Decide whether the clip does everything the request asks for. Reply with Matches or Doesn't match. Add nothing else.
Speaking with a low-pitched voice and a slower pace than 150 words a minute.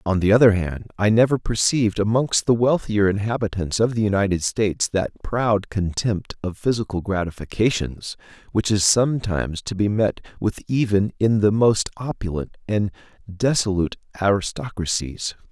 Matches